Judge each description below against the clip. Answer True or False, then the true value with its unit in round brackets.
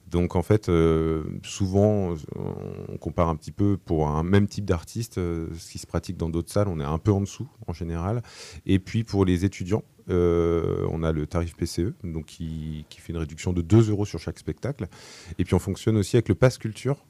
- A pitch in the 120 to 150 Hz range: False (90 Hz)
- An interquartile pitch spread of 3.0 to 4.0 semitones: True (3.7 semitones)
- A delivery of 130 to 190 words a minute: False (220 wpm)